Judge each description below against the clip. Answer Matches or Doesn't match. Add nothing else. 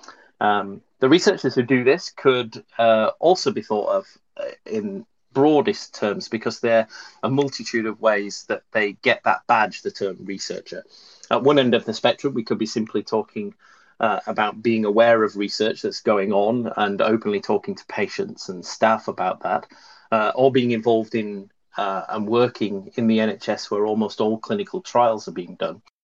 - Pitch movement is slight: Doesn't match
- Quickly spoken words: Doesn't match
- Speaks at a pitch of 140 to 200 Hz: Doesn't match